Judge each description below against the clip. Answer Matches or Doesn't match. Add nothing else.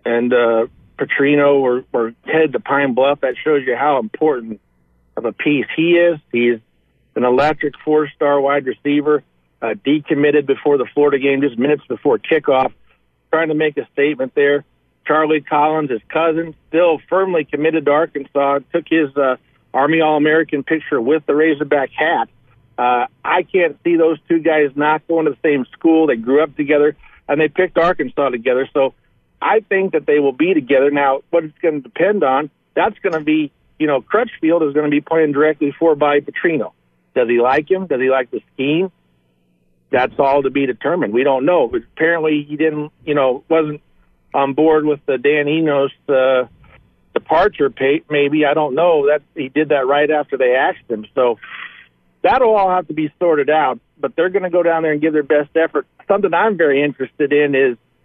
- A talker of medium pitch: Matches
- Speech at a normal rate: Matches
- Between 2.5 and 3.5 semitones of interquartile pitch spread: Matches